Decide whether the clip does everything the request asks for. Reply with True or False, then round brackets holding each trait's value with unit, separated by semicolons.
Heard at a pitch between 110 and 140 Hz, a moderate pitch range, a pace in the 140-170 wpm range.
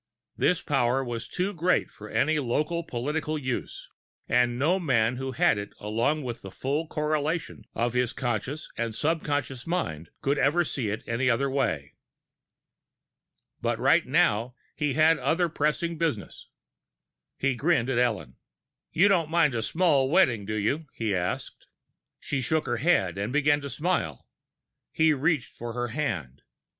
True (135 Hz; 4.9 semitones; 150 wpm)